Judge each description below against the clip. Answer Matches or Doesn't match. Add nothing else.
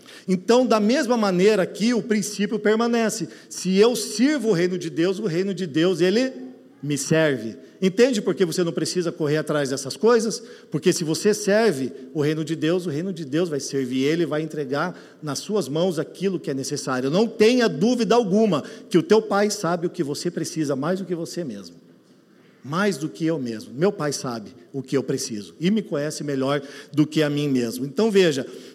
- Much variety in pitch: Matches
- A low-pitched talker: Doesn't match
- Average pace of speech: Doesn't match